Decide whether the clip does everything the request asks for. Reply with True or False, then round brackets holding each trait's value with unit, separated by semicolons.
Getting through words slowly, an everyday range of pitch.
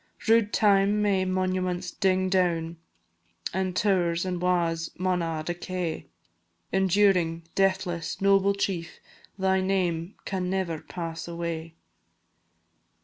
False (105 wpm; 2.2 semitones)